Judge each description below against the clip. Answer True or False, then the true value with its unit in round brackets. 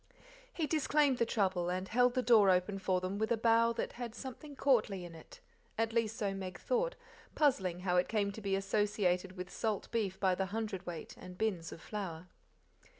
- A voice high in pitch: True (205 Hz)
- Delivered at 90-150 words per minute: False (195 wpm)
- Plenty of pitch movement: False (3.9 semitones)